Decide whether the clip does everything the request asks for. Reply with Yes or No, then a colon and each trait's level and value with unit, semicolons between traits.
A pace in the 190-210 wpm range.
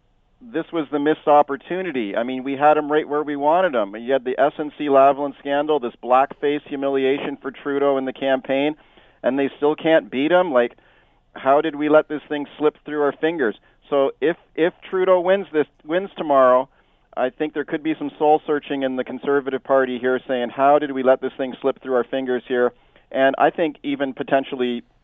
Yes: average, 200 wpm